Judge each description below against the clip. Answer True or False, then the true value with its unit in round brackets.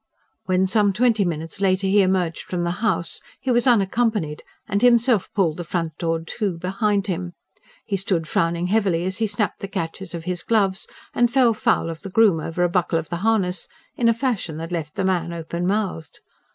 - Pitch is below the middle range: False (185 Hz)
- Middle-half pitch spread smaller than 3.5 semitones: False (3.8 semitones)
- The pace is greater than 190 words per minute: True (200 wpm)